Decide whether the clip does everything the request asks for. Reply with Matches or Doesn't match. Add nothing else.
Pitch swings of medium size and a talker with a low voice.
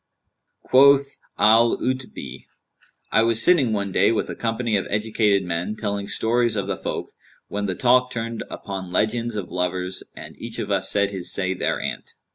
Matches